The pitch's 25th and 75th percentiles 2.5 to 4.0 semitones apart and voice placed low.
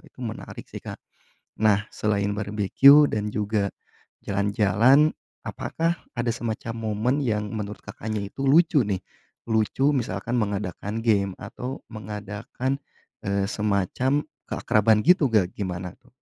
Yes: average, 3.5 semitones; low, 110 Hz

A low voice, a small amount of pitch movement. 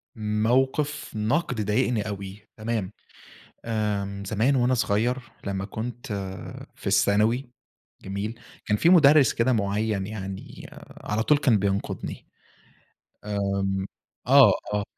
No: low, 110 Hz; average, 3.8 semitones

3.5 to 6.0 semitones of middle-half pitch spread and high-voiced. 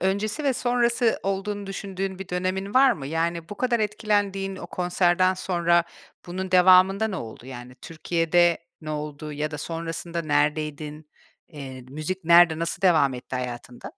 No: average, 4.1 semitones; medium, 175 Hz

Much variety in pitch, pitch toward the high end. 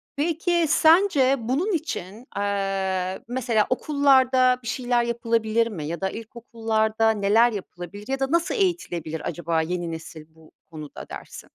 Yes: wide, 5.7 semitones; high, 225 Hz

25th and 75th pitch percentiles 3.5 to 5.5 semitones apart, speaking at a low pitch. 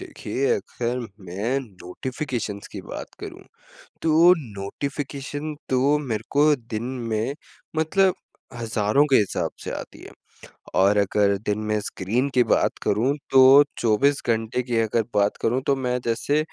Yes: average, 4.8 semitones; low, 120 Hz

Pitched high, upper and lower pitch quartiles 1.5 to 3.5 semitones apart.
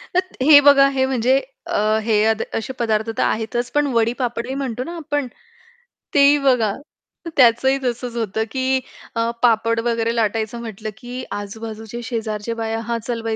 Yes: high, 235 Hz; average, 2.7 semitones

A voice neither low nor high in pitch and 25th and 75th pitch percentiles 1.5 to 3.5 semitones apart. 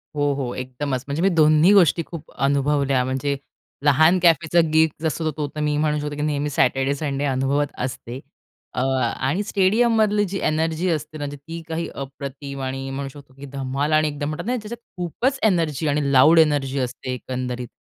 Yes: medium, 145 Hz; average, 3.1 semitones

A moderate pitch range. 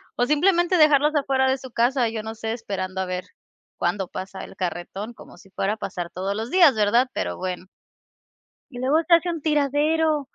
No: wide, 7.4 semitones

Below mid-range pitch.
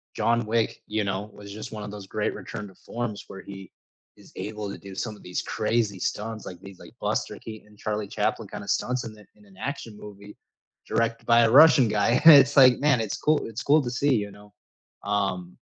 Yes: low, 105 Hz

